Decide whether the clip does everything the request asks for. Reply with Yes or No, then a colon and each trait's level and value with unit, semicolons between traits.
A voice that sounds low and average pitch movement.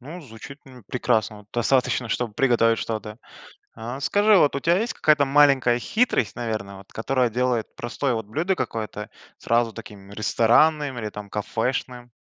Yes: low, 120 Hz; average, 3.9 semitones